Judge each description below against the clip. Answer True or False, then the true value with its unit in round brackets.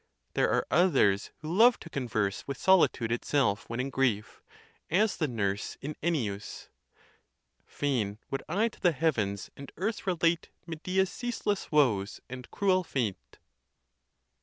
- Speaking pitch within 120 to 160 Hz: True (140 Hz)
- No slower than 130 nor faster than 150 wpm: True (135 wpm)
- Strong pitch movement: True (8.1 semitones)